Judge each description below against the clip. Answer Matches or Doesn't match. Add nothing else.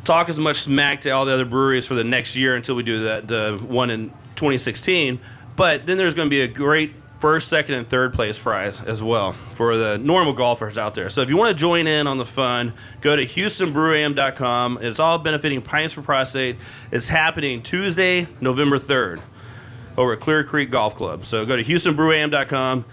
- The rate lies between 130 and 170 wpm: Doesn't match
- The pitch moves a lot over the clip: Doesn't match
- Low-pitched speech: Matches